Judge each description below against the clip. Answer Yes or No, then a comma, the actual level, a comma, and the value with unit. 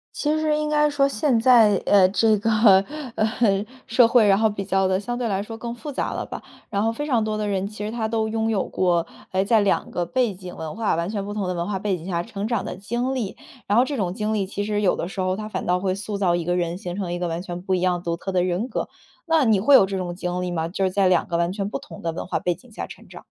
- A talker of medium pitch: No, high, 200 Hz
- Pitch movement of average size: Yes, average, 3.7 semitones